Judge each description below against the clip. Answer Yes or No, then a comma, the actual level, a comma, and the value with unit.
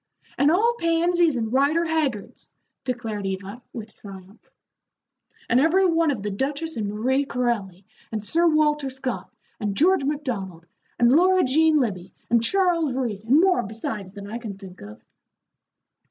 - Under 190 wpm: Yes, average, 155 wpm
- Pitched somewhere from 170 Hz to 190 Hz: No, very high, 255 Hz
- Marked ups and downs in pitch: Yes, wide, 7.4 semitones